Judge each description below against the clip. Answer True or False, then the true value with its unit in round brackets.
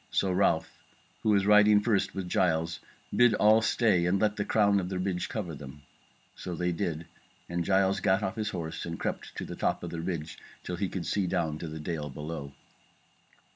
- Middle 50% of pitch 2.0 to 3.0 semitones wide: False (3.6 semitones)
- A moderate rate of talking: False (210 wpm)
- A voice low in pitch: True (90 Hz)